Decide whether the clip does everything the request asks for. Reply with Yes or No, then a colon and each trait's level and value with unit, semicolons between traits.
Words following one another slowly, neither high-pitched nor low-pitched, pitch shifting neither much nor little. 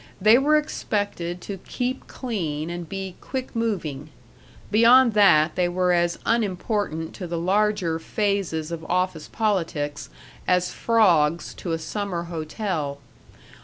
Yes: slow, 130 wpm; medium, 180 Hz; average, 4.5 semitones